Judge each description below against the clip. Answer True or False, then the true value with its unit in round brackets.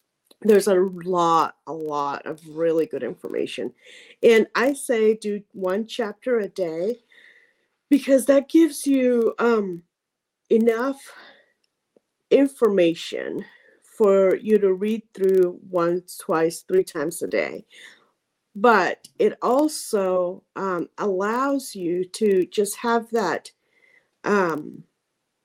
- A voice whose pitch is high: True (220 Hz)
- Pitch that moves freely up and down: True (7.1 semitones)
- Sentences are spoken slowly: True (110 wpm)